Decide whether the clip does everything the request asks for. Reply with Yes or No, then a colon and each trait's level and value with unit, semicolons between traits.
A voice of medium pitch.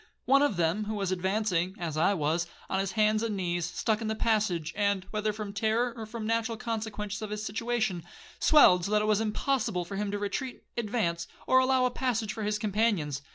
No: high, 210 Hz